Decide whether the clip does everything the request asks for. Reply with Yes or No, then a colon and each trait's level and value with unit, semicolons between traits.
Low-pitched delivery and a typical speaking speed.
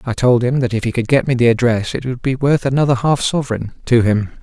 No: low, 125 Hz; fast, 270 wpm